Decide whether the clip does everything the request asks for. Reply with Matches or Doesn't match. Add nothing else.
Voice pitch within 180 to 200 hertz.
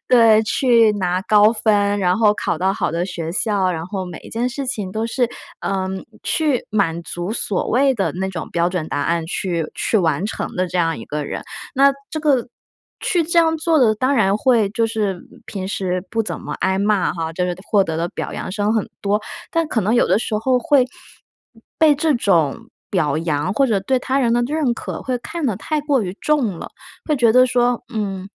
Doesn't match